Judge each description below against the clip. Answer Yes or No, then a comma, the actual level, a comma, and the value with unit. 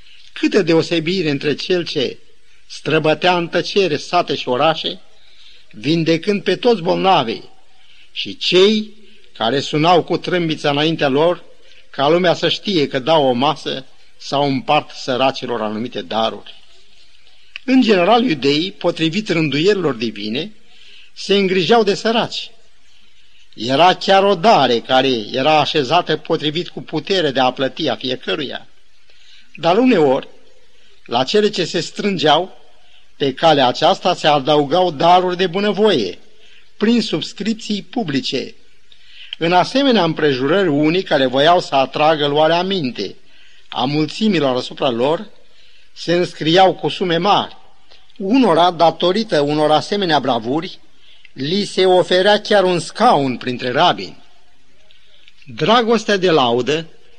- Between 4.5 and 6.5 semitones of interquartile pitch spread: Yes, average, 5.1 semitones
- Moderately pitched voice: Yes, medium, 170 Hz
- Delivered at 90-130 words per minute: Yes, average, 120 wpm